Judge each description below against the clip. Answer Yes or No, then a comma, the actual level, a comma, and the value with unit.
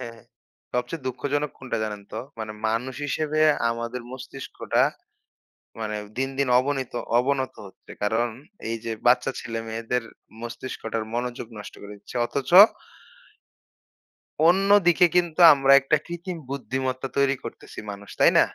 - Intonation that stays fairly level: No, average, 3.4 semitones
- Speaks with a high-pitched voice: No, low, 130 Hz